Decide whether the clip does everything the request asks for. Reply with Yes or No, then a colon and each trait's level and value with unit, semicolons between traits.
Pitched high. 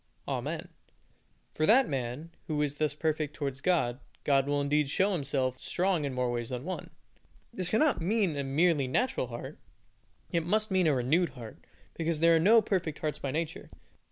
No: medium, 155 Hz